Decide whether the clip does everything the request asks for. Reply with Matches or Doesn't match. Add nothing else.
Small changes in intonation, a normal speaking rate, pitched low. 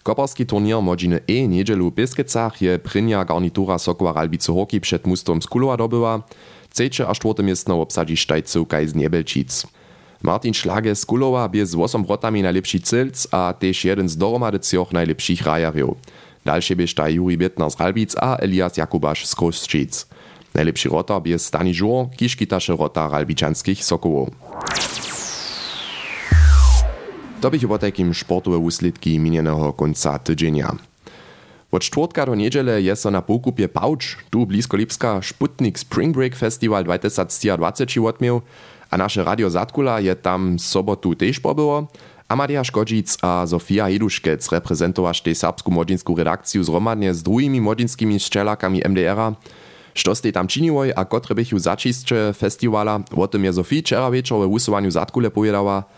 Doesn't match